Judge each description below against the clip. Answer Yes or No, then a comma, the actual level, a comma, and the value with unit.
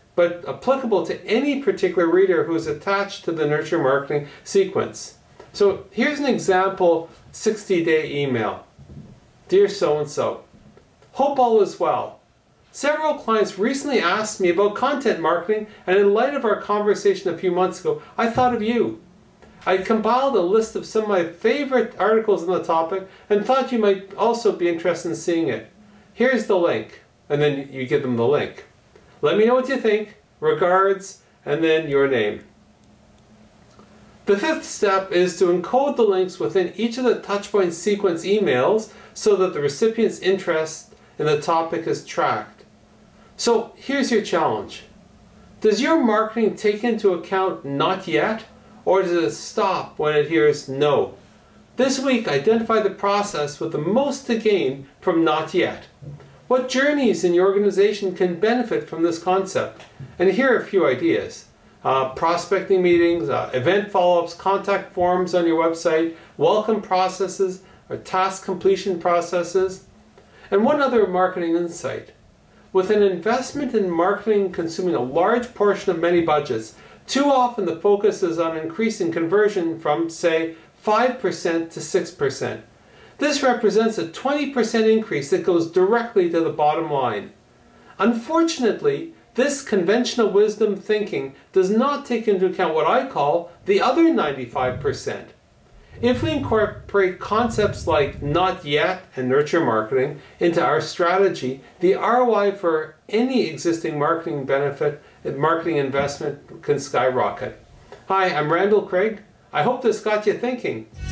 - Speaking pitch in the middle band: No, high, 195 Hz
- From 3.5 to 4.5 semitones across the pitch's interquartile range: No, average, 5.2 semitones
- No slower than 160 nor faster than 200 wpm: No, average, 150 wpm